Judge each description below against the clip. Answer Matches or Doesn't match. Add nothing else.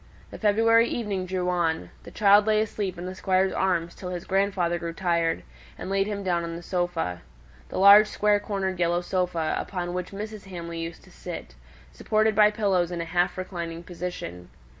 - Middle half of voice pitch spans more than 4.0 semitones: Doesn't match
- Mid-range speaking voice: Matches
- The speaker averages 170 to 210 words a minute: Matches